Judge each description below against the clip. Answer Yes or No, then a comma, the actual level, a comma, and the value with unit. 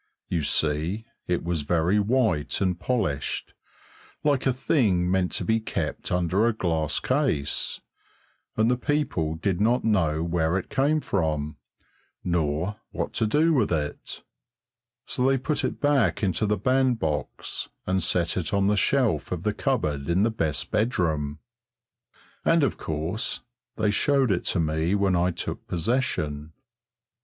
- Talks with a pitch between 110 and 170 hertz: No, very low, 95 Hz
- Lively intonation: Yes, wide, 6.6 semitones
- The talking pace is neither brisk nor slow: Yes, average, 150 wpm